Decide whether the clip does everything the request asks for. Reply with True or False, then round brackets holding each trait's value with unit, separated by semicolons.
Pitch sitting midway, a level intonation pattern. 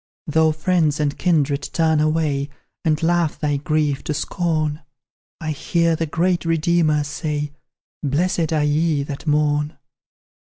True (155 Hz; 1.8 semitones)